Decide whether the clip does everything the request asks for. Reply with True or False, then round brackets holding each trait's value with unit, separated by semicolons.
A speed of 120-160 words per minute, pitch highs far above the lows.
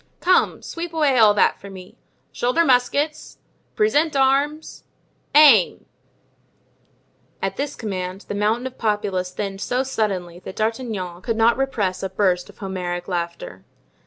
True (135 wpm; 6.3 semitones)